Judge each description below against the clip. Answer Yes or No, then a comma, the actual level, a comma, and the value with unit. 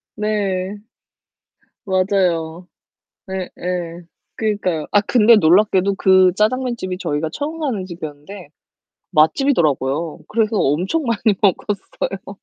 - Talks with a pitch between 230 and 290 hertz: No, high, 190 Hz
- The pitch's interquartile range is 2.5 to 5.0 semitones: Yes, average, 3.7 semitones